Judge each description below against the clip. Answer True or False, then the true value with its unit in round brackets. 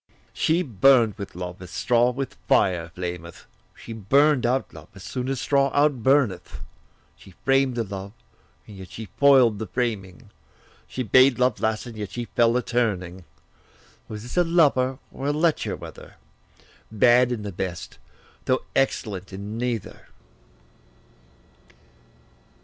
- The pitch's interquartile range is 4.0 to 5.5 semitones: True (5.1 semitones)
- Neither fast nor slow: True (145 wpm)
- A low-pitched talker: True (115 Hz)